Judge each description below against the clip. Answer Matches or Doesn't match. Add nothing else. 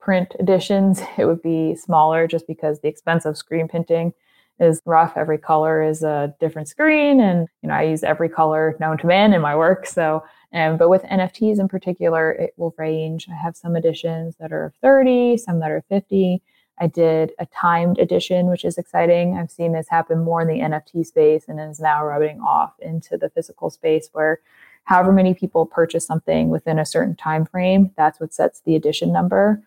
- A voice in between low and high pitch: Matches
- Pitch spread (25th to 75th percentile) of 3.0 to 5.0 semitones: Doesn't match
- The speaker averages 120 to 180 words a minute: Doesn't match